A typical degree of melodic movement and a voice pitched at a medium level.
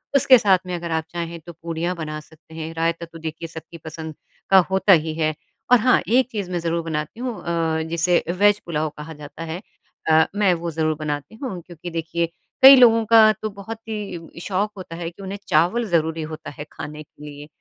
Yes: average, 3.4 semitones; medium, 170 Hz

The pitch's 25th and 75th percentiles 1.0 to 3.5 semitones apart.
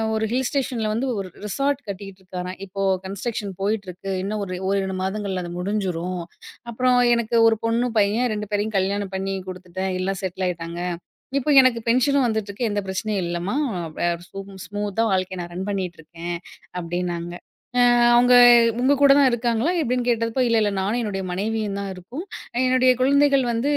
No: average, 4.2 semitones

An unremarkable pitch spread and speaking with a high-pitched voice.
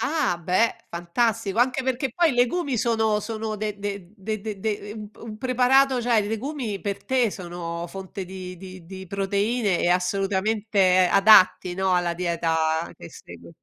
Yes: average, 4.0 semitones; high, 205 Hz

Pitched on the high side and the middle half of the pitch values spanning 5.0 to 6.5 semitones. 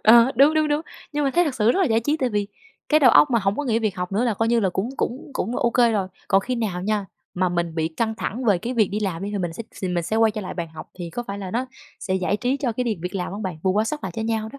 No: high, 220 Hz; average, 4.4 semitones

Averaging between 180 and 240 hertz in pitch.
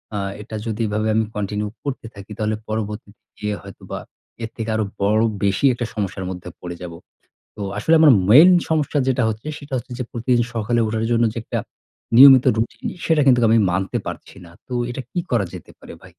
No: low, 110 Hz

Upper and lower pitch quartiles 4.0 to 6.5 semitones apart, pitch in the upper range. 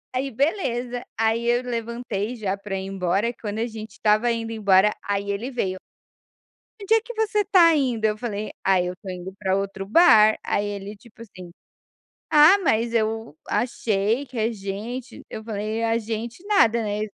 No: average, 3.2 semitones; high, 225 Hz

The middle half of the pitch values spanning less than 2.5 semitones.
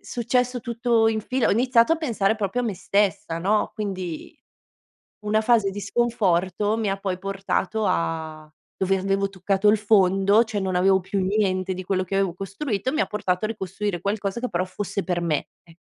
No: average, 2.8 semitones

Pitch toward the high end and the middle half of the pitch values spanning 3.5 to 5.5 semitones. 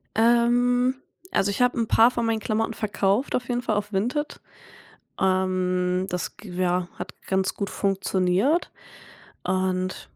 Yes: high, 200 Hz; average, 4.2 semitones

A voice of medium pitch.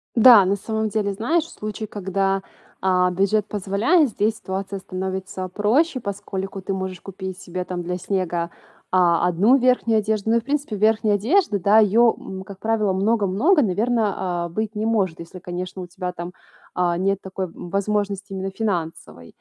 No: high, 195 Hz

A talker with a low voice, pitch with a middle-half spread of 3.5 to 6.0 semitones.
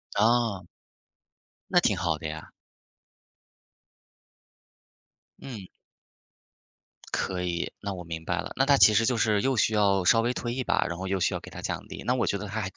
Yes: low, 100 Hz; average, 4.4 semitones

